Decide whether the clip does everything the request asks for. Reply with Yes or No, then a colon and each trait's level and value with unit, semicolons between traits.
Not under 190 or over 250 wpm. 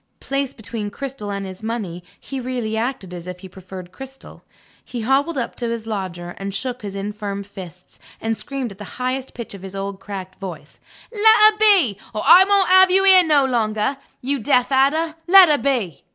Yes: average, 195 wpm